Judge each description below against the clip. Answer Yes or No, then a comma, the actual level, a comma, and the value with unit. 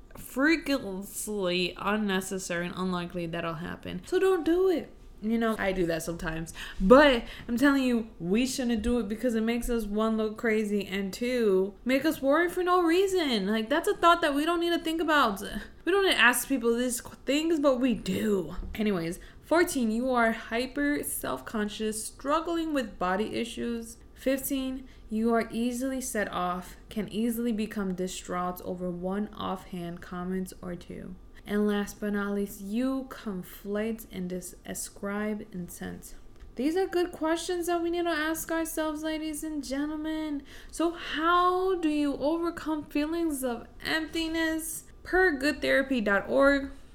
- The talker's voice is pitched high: Yes, high, 235 Hz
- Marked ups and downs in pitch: Yes, wide, 7.4 semitones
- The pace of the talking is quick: No, average, 155 wpm